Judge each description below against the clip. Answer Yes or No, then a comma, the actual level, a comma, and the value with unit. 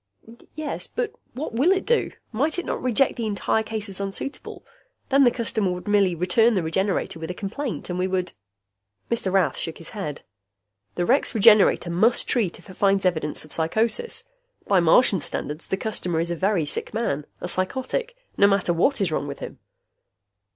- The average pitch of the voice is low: No, high, 195 Hz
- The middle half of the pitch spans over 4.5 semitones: Yes, average, 5.1 semitones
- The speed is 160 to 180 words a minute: No, average, 190 wpm